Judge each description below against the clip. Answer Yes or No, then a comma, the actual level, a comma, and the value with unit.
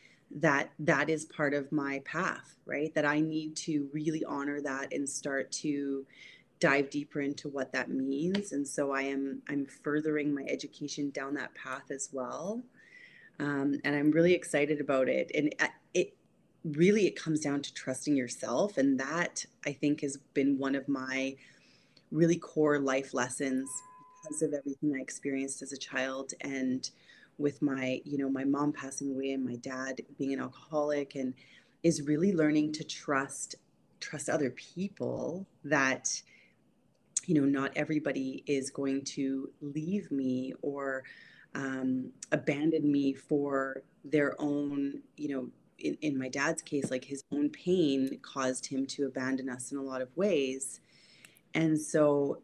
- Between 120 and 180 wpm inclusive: Yes, average, 160 wpm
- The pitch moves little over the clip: Yes, narrow, 2.0 semitones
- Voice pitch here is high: No, medium, 140 Hz